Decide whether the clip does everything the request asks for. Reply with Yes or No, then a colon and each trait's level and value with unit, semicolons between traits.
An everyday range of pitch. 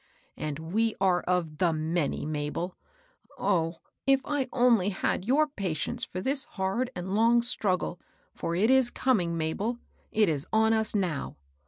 No: wide, 5.8 semitones